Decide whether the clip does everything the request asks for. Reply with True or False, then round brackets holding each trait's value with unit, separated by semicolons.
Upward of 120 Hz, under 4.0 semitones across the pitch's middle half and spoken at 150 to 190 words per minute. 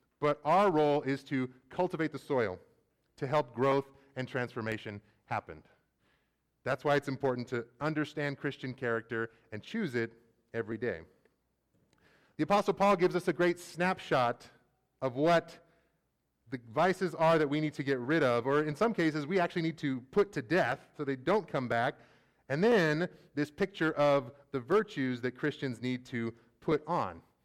False (140 Hz; 5.0 semitones; 165 wpm)